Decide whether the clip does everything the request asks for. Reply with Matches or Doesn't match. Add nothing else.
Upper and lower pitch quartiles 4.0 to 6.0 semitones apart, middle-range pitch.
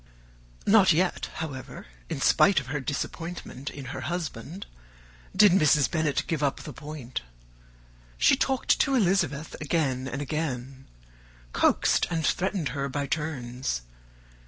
Matches